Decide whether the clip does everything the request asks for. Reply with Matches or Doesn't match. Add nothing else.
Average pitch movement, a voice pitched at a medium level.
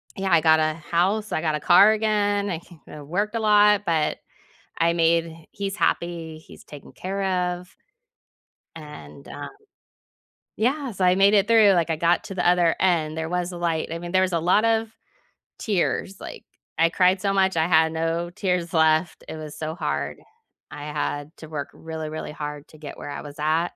Matches